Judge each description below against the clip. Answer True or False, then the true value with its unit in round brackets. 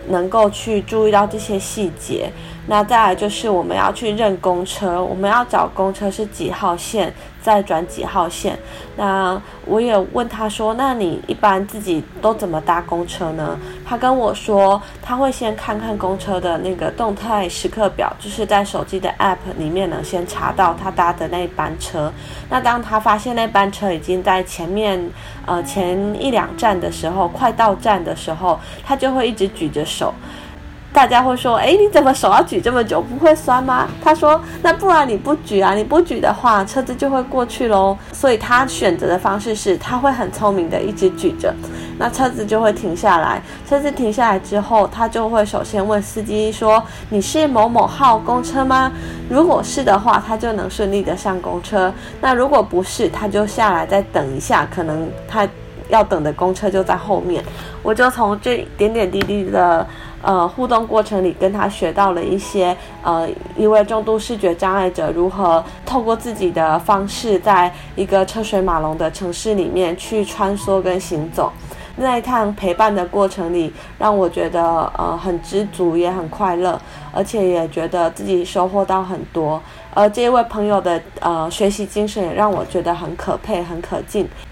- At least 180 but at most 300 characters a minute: True (265 characters per minute)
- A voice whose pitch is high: True (200 Hz)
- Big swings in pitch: False (3.6 semitones)